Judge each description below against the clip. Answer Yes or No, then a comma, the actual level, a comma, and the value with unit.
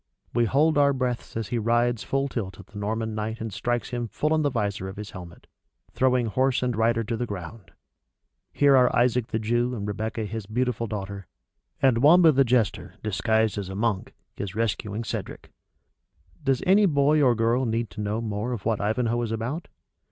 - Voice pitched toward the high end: No, low, 115 Hz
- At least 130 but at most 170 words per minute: No, average, 195 wpm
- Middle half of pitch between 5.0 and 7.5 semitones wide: No, average, 3.0 semitones